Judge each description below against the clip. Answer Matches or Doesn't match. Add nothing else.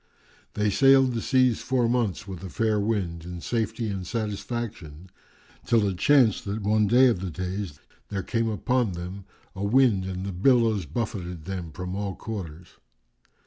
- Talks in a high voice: Doesn't match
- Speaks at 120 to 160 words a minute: Doesn't match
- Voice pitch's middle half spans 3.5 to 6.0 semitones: Matches